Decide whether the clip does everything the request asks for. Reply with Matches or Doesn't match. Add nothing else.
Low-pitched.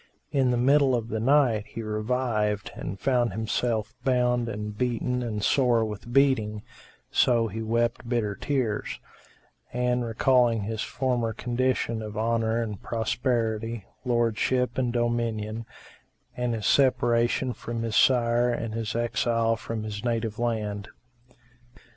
Matches